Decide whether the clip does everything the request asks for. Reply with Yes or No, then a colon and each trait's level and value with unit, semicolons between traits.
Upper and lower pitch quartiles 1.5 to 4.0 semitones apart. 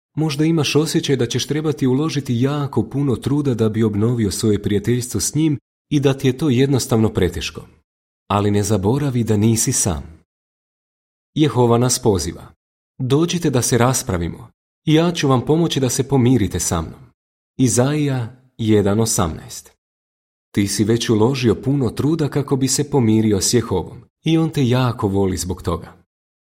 No: average, 5.3 semitones